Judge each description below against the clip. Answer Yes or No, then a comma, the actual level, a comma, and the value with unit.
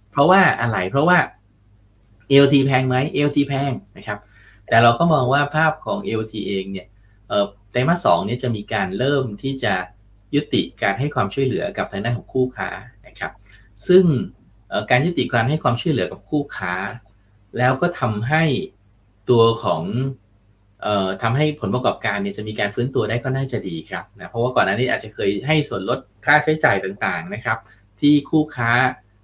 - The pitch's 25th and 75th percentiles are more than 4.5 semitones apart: Yes, average, 5.2 semitones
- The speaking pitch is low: Yes, low, 120 Hz